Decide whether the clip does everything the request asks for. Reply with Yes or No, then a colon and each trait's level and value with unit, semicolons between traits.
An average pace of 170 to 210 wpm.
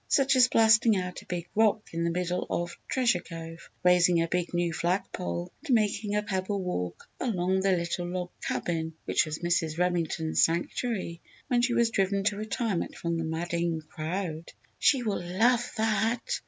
Yes: average, 175 wpm